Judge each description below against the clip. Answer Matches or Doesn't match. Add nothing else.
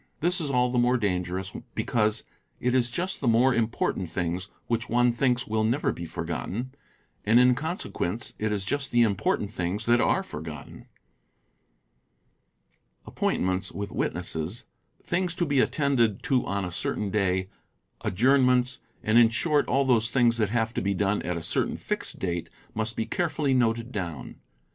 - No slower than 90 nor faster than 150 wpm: Doesn't match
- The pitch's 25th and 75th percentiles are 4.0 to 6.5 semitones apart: Matches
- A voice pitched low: Matches